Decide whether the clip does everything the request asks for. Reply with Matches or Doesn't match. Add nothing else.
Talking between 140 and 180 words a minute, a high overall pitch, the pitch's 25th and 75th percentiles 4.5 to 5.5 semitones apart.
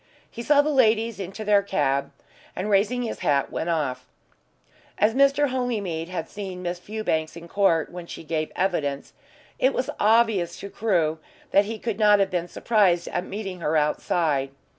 Matches